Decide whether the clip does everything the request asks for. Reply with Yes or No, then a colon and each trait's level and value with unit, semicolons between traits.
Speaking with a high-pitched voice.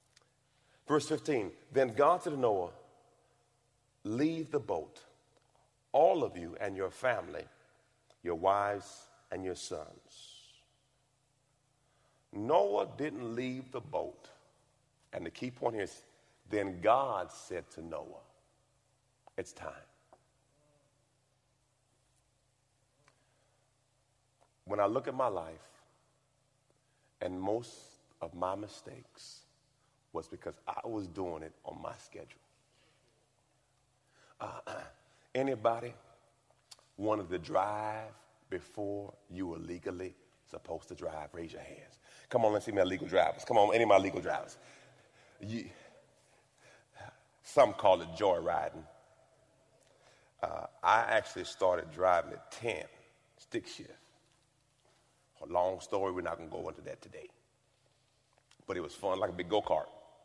No: low, 125 Hz